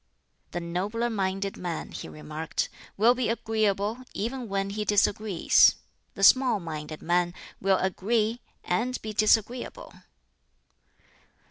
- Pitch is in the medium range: No, high, 200 Hz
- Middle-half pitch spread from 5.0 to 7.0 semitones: No, average, 4.0 semitones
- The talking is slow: Yes, slow, 115 wpm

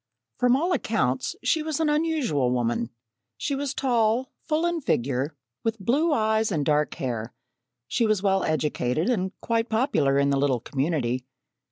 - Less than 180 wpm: Yes, average, 160 wpm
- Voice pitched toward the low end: No, high, 205 Hz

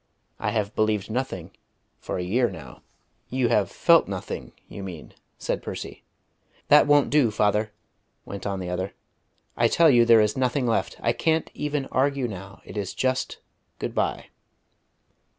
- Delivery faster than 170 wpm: No, average, 160 wpm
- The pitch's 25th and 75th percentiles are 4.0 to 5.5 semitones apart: Yes, average, 4.7 semitones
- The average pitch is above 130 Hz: No, low, 115 Hz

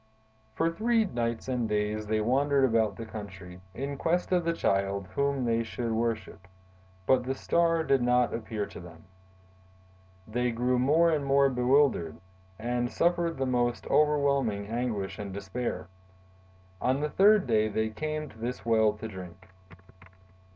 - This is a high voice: No, low, 120 Hz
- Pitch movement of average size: Yes, average, 4.5 semitones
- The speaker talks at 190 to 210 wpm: No, average, 150 wpm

